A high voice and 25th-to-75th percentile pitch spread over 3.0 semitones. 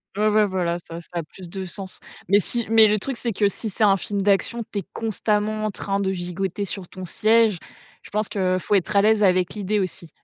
No: high, 200 Hz; narrow, 2.5 semitones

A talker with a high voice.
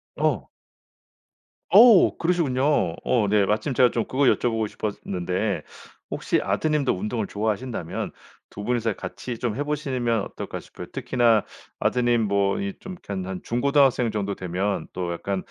No: low, 115 Hz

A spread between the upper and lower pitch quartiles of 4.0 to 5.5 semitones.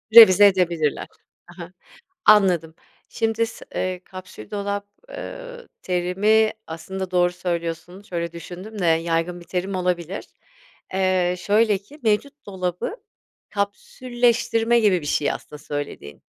No: average, 3.6 semitones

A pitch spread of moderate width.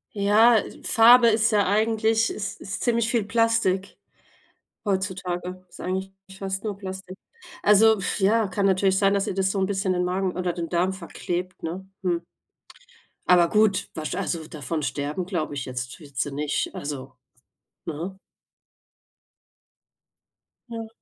Yes: average, 3.1 semitones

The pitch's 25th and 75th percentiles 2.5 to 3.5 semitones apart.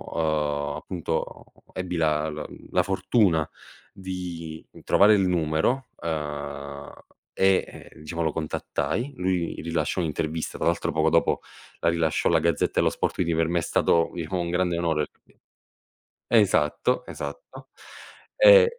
Yes: average, 2.8 semitones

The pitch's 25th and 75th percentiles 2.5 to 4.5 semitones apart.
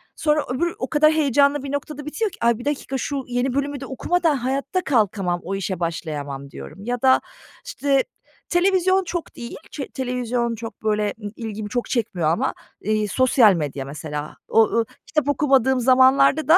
No: average, 5.3 semitones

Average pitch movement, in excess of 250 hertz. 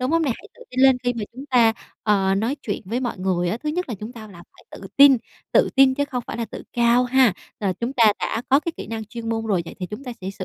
No: average, 3.8 semitones; high, 235 Hz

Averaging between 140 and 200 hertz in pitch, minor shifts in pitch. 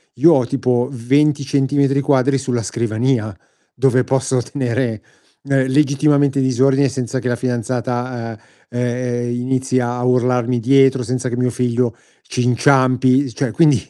No: low, 125 Hz; narrow, 1.9 semitones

